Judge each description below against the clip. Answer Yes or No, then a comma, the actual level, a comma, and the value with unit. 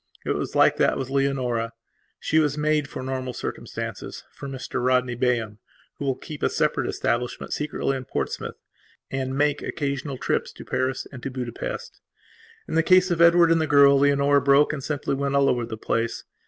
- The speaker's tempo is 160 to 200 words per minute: Yes, average, 180 wpm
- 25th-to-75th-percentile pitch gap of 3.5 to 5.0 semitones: No, narrow, 2.5 semitones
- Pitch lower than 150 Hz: Yes, medium, 140 Hz